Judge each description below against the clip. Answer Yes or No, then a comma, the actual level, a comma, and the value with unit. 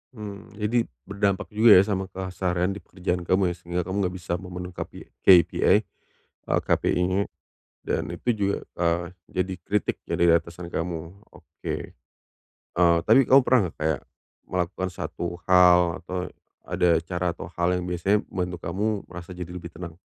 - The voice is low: Yes, very low, 90 Hz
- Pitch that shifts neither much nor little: No, narrow, 2.0 semitones